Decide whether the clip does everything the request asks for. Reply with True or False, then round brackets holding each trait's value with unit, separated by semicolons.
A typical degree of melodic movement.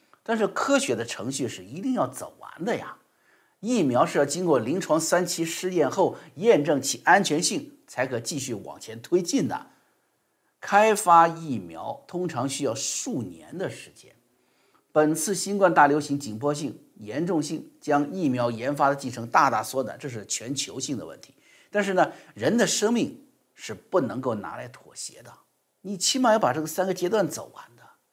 False (6.2 semitones)